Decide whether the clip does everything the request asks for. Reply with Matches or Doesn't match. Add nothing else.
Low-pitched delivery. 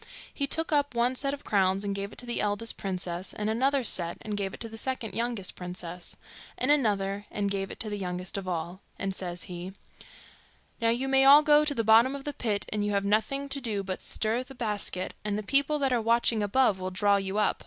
Doesn't match